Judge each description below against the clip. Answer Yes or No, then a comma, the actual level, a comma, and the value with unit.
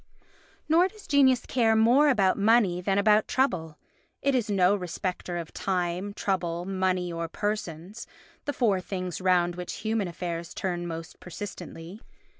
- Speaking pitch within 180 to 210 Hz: Yes, high, 190 Hz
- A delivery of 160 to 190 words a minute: No, average, 145 wpm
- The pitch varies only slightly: No, average, 4.0 semitones